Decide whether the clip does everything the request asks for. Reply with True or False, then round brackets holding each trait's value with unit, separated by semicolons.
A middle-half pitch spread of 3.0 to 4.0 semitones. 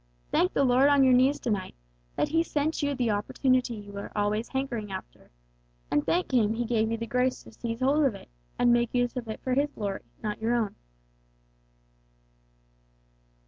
True (3.5 semitones)